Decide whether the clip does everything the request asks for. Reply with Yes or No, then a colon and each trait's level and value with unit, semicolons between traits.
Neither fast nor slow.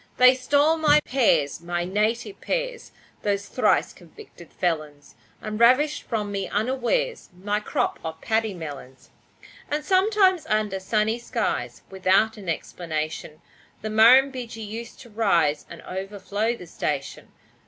No: slow, 130 wpm